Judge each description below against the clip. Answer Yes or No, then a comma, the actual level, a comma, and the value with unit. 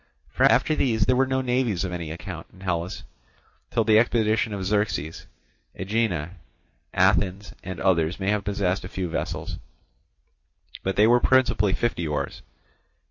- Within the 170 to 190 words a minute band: No, average, 150 wpm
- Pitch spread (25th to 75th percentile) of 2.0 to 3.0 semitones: No, average, 3.8 semitones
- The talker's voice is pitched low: Yes, low, 100 Hz